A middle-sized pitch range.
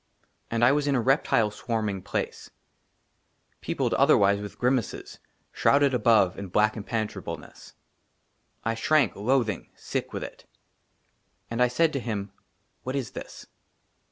Yes: average, 3.9 semitones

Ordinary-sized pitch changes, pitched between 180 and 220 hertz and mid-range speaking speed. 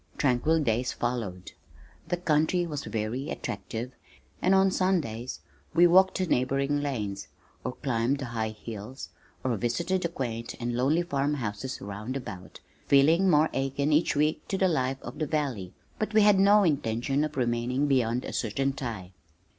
No: average, 5.0 semitones; low, 135 Hz; average, 160 wpm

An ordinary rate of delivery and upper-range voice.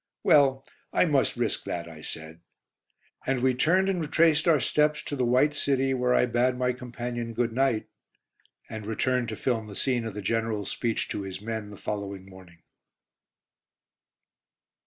No: average, 165 wpm; low, 120 Hz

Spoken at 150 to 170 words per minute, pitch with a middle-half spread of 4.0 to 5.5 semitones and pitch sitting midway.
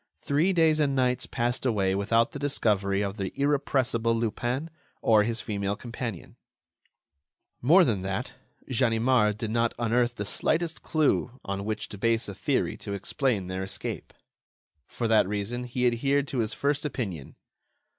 No: average, 155 wpm; average, 4.5 semitones; low, 115 Hz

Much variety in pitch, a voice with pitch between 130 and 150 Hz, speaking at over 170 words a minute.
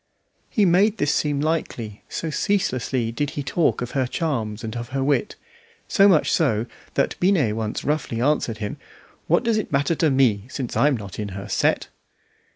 Yes: wide, 5.9 semitones; low, 135 Hz; average, 180 wpm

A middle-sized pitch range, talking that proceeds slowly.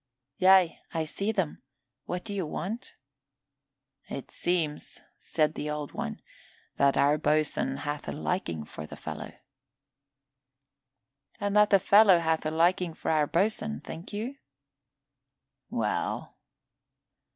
Yes: average, 4.7 semitones; slow, 125 wpm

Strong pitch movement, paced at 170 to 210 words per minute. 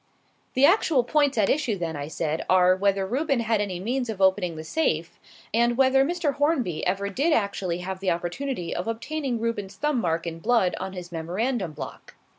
Yes: wide, 6.7 semitones; average, 190 wpm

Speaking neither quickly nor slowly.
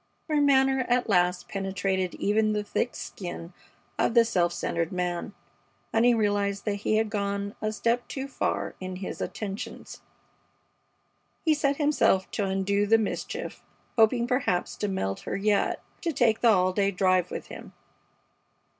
Yes: average, 155 wpm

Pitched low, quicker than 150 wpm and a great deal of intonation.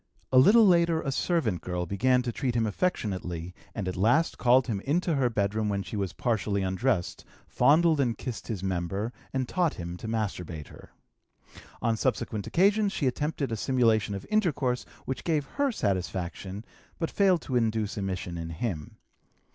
Yes: low, 115 Hz; average, 170 wpm; wide, 6.7 semitones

